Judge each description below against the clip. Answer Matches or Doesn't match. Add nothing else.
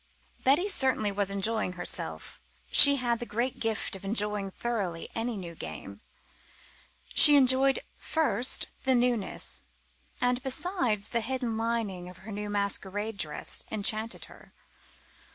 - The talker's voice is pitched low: Doesn't match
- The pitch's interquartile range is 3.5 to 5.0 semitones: Matches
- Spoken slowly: Matches